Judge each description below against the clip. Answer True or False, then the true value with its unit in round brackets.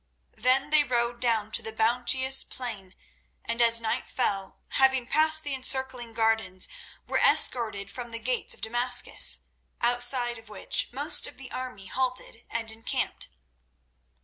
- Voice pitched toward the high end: True (240 Hz)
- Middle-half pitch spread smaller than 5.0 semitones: True (2.5 semitones)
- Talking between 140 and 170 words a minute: True (145 wpm)